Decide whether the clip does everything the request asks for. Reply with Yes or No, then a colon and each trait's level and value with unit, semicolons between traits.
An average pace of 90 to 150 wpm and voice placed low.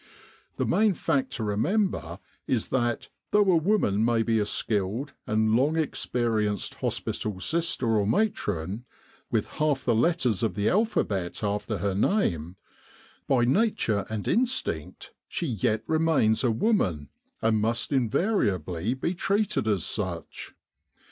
Yes: slow, 135 wpm; low, 115 Hz